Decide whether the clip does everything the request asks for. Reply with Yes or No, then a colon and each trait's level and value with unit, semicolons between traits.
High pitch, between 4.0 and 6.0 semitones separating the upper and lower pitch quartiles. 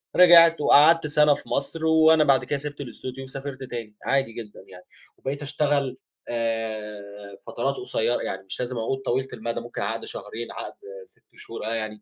No: low, 130 Hz; average, 4.5 semitones